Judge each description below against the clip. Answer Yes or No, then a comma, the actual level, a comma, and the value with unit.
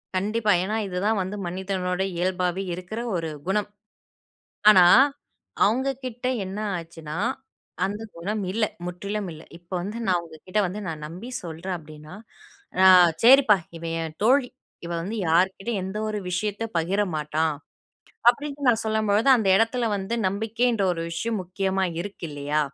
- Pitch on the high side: Yes, high, 195 Hz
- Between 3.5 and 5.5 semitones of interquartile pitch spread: Yes, average, 3.8 semitones